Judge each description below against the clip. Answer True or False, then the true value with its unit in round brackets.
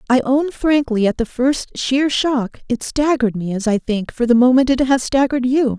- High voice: True (255 Hz)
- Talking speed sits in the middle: False (220 wpm)